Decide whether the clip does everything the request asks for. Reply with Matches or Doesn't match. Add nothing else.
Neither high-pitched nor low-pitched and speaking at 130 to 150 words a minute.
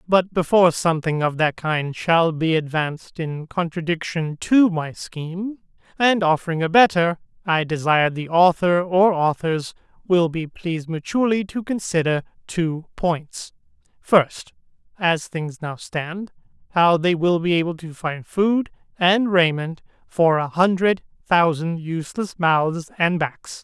Matches